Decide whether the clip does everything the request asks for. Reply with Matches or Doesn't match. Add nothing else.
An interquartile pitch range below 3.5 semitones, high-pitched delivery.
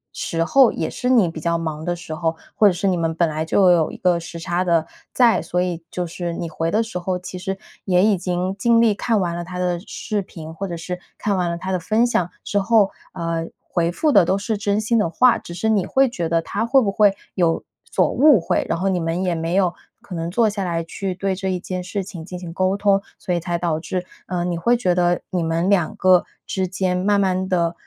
Doesn't match